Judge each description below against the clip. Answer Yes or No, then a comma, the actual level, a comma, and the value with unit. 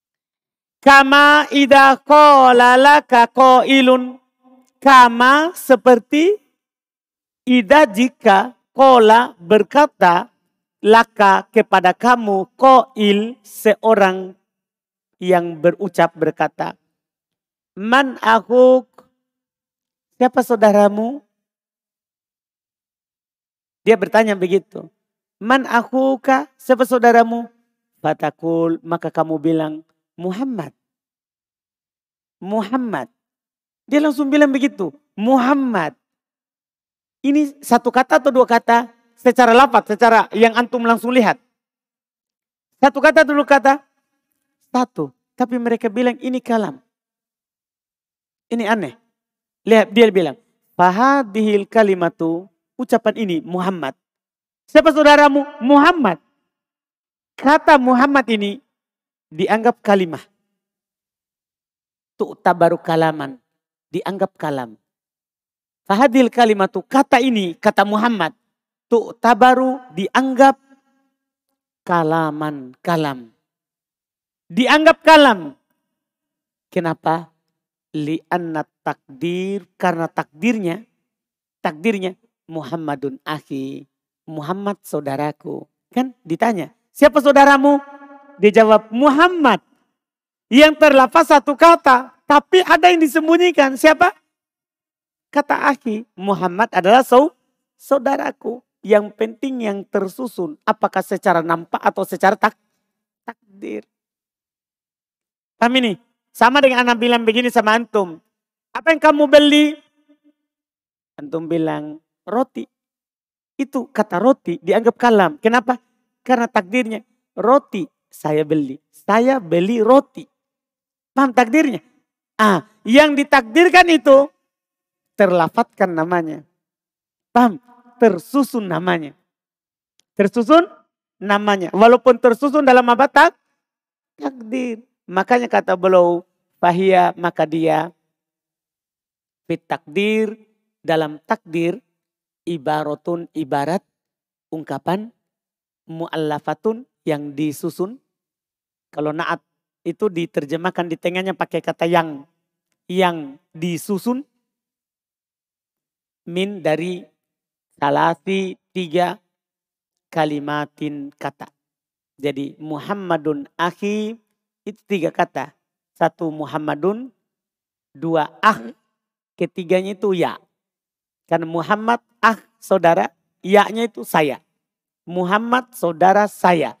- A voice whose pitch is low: No, high, 215 Hz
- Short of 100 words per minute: Yes, slow, 85 wpm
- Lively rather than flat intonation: Yes, wide, 6.7 semitones